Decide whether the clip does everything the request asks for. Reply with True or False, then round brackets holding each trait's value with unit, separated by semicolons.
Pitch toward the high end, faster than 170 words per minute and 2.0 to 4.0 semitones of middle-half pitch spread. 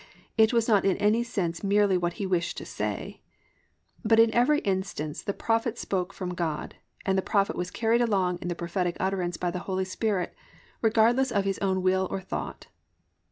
True (195 Hz; 190 wpm; 3.5 semitones)